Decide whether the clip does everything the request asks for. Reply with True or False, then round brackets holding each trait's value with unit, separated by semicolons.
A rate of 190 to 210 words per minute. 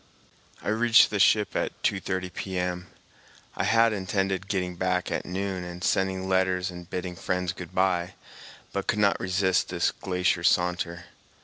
False (150 wpm)